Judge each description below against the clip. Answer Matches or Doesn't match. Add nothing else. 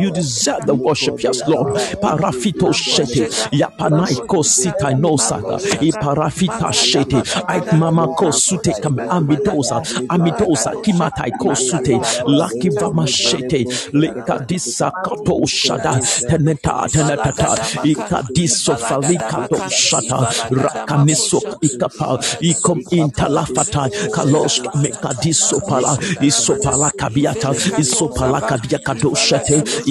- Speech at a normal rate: Doesn't match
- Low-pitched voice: Doesn't match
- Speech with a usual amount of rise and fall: Matches